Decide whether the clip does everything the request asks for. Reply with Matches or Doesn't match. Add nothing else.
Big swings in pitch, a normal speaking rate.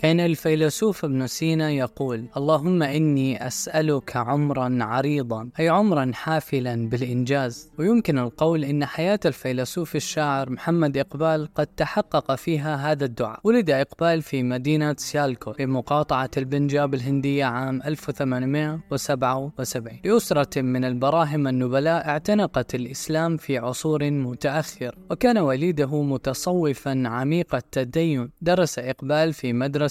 Doesn't match